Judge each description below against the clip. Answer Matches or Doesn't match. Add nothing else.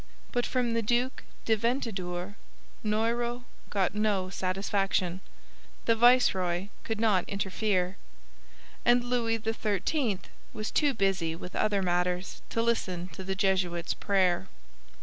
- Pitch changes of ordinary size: Matches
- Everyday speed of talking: Doesn't match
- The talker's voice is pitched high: Matches